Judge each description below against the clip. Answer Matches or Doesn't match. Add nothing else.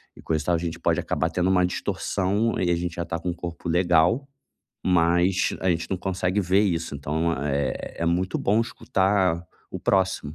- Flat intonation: Matches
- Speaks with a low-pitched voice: Matches